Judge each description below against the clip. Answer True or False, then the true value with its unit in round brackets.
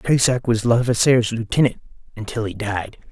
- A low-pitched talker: True (115 Hz)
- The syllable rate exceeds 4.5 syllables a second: True (5.3 syllables/s)